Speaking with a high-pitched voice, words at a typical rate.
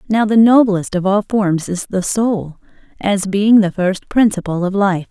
Yes: high, 200 Hz; average, 190 wpm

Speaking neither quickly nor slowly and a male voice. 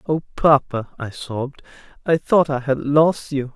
Yes: average, 170 wpm; male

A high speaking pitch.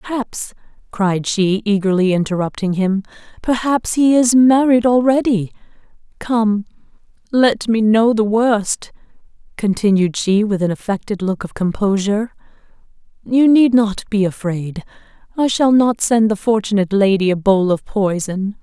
Yes: high, 210 Hz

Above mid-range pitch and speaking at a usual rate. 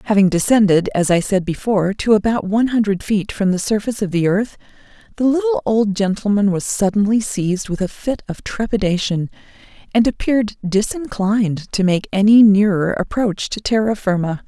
Yes: high, 205 Hz; average, 165 wpm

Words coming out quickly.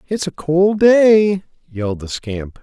No: average, 160 wpm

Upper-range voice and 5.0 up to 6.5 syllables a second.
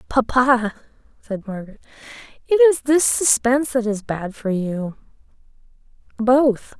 No: high, 240 Hz; 4.2 syllables/s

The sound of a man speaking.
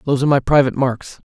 Yes: male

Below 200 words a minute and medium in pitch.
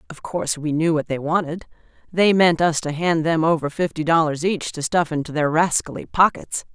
No: fast, 205 wpm; medium, 160 Hz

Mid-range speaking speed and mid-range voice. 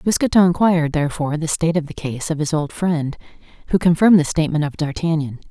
Yes: average, 195 wpm; medium, 160 Hz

